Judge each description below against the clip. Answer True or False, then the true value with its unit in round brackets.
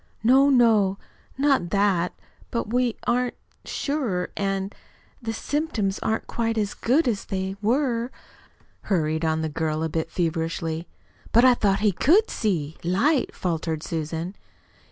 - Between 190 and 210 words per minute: False (140 wpm)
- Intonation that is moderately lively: False (6.3 semitones)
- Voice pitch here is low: False (200 Hz)